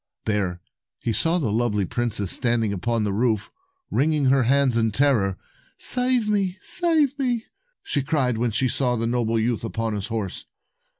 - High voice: No, low, 120 Hz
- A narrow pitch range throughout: No, average, 4.8 semitones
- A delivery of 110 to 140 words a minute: No, average, 165 wpm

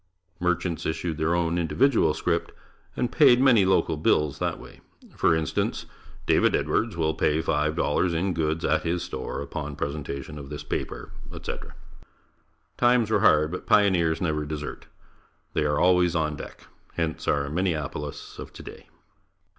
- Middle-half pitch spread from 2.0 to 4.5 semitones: Yes, average, 2.9 semitones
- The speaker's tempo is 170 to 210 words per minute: No, average, 150 wpm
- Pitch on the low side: Yes, very low, 80 Hz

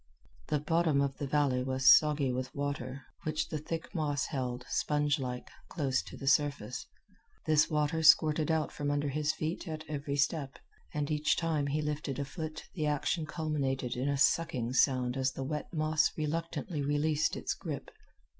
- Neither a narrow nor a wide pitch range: No, narrow, 2.2 semitones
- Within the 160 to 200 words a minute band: Yes, average, 170 wpm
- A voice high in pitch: No, medium, 145 Hz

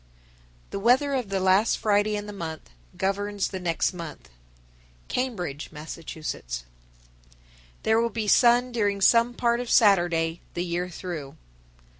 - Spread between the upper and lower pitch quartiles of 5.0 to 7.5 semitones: Yes, average, 5.3 semitones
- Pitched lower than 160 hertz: No, high, 195 Hz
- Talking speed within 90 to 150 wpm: Yes, average, 140 wpm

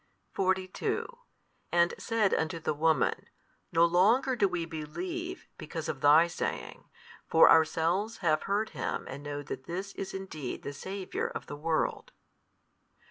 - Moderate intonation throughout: Yes, average, 4.1 semitones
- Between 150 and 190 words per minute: No, average, 140 wpm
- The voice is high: No, medium, 170 Hz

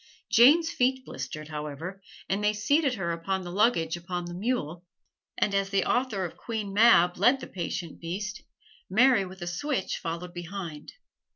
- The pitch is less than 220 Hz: Yes, high, 190 Hz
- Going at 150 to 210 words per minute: Yes, average, 165 wpm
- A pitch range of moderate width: Yes, average, 5.0 semitones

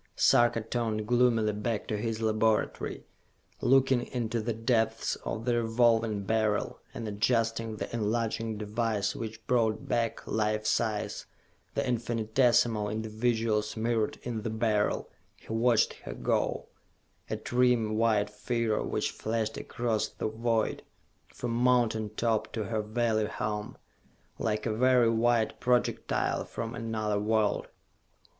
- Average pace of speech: No, slow, 125 wpm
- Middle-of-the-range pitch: No, low, 110 Hz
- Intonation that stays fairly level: Yes, narrow, 1.5 semitones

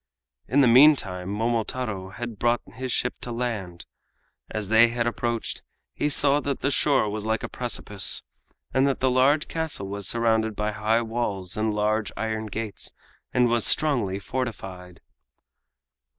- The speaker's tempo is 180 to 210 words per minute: No, average, 150 wpm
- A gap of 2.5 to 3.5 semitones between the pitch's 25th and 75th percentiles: Yes, average, 3.2 semitones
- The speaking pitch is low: Yes, low, 115 Hz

